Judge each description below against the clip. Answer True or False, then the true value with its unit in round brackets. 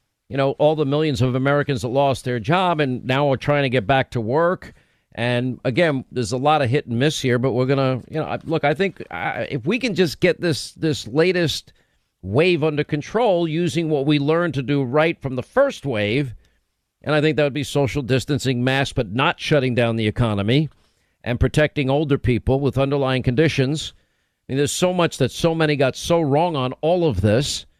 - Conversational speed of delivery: False (210 wpm)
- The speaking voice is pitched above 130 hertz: True (140 Hz)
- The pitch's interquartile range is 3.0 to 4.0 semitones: True (3.4 semitones)